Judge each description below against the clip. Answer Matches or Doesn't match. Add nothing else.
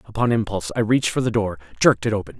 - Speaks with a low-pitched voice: Matches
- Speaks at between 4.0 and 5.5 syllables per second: Doesn't match